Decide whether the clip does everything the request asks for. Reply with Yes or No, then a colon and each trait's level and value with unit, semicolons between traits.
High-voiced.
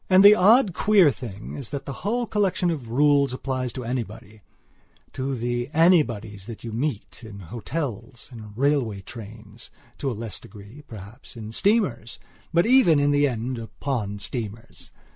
No: low, 125 Hz